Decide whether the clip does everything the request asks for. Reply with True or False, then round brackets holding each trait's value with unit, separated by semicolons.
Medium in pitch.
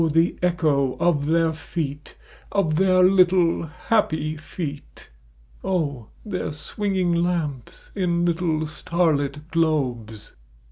True (165 Hz)